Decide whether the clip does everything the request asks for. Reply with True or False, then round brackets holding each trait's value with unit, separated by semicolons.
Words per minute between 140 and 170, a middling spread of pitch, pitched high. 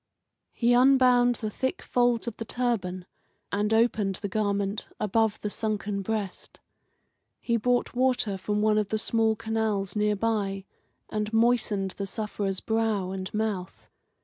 False (145 wpm; 2.3 semitones; 215 Hz)